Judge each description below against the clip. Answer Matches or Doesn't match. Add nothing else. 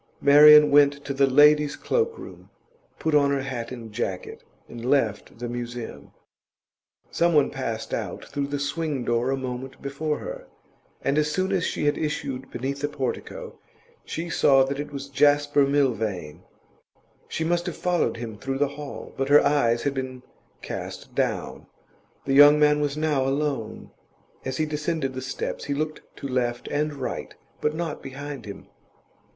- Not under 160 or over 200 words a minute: Matches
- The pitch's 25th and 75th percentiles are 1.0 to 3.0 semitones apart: Matches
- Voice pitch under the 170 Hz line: Matches